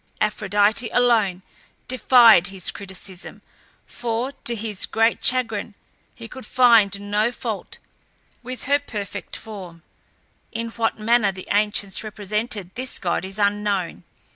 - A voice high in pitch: Yes, high, 215 Hz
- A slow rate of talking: Yes, slow, 120 wpm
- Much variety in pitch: No, average, 2.8 semitones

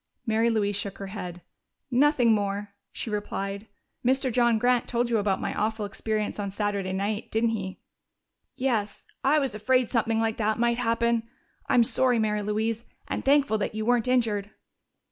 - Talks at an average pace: Yes, average, 165 wpm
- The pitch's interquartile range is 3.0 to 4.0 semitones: No, narrow, 2.6 semitones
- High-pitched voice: Yes, high, 220 Hz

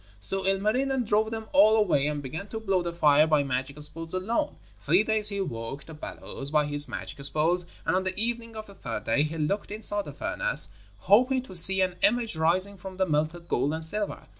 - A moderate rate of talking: No, fast, 215 wpm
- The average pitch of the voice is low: No, medium, 185 Hz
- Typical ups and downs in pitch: No, wide, 5.9 semitones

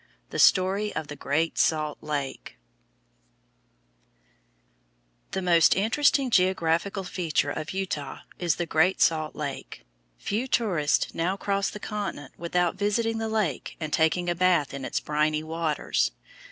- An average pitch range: Yes, average, 4.3 semitones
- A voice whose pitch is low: No, medium, 175 Hz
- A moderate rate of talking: No, slow, 130 wpm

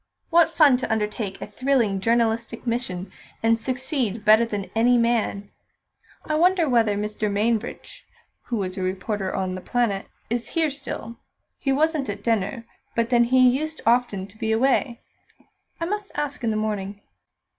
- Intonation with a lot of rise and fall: No, average, 3.9 semitones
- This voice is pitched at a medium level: No, high, 230 Hz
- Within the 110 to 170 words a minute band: Yes, average, 160 wpm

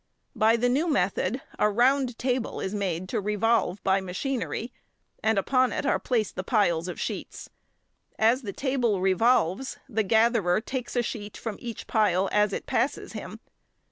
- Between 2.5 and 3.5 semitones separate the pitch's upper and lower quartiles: No, average, 4.0 semitones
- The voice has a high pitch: Yes, high, 220 Hz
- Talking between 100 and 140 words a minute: No, average, 165 wpm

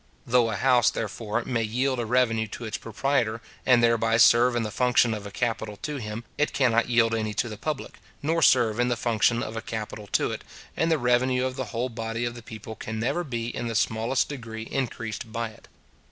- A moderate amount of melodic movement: No, narrow, 2.0 semitones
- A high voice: No, low, 115 Hz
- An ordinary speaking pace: No, fast, 220 wpm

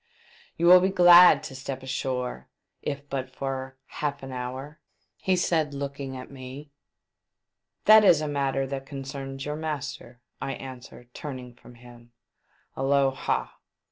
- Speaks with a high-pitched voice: No, low, 135 Hz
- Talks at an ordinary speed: Yes, average, 160 wpm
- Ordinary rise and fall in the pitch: No, narrow, 2.2 semitones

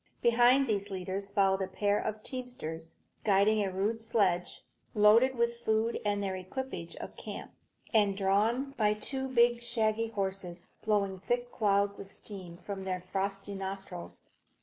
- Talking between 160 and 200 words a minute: No, average, 150 wpm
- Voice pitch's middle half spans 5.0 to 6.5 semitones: No, average, 3.0 semitones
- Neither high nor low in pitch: No, high, 205 Hz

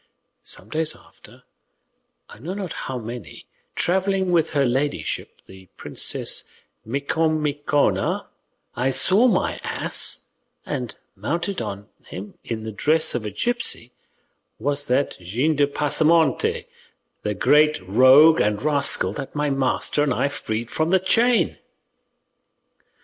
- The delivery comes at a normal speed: No, slow, 125 wpm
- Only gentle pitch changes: No, average, 4.8 semitones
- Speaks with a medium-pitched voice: Yes, medium, 145 Hz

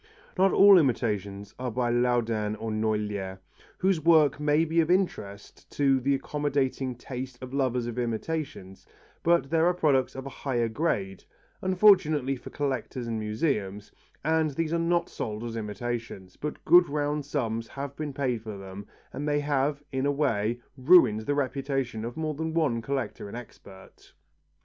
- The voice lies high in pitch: No, low, 130 Hz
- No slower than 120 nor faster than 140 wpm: No, average, 165 wpm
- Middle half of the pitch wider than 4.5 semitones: Yes, average, 5.0 semitones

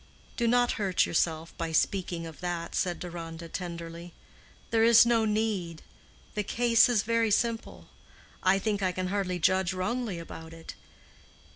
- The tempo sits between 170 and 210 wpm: No, average, 150 wpm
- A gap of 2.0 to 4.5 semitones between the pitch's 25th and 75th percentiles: No, average, 4.9 semitones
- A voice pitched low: No, medium, 185 Hz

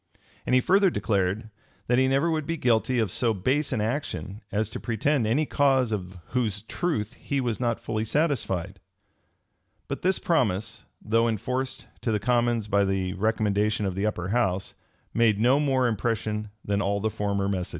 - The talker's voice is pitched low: Yes, low, 110 Hz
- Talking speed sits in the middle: Yes, average, 175 wpm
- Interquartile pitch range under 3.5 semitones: No, average, 4.0 semitones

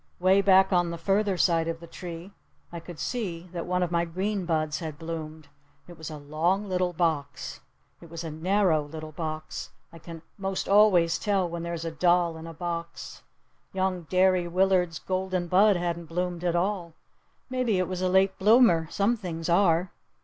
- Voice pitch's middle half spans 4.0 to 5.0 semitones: No, narrow, 2.4 semitones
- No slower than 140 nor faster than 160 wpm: No, average, 185 wpm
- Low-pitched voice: No, medium, 175 Hz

